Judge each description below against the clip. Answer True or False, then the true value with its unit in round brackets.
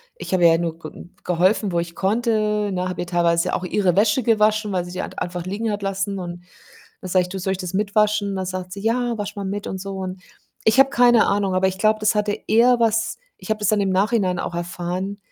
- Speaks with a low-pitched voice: False (195 Hz)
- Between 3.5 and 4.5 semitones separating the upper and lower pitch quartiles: False (2.8 semitones)